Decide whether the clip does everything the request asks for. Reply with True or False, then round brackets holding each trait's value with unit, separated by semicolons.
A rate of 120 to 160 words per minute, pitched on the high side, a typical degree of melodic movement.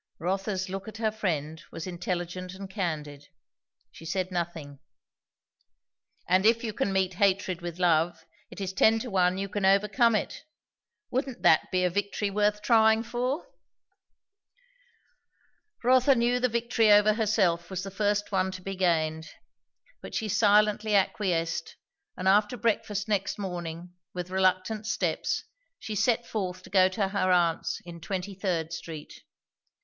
True (150 wpm; 195 Hz; 3.1 semitones)